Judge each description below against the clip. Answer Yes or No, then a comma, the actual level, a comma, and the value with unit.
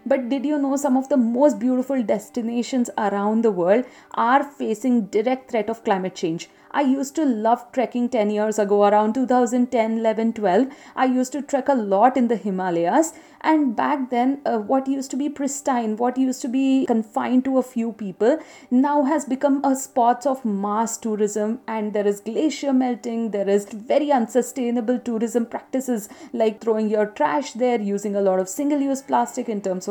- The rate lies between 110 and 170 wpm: No, average, 185 wpm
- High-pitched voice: Yes, high, 245 Hz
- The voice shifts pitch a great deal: No, average, 3.7 semitones